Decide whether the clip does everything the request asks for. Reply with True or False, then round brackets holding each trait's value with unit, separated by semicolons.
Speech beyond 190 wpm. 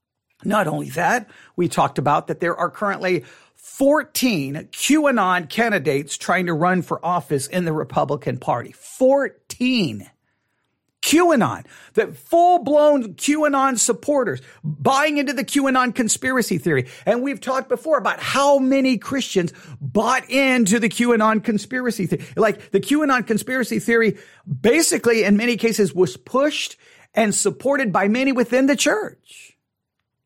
False (135 wpm)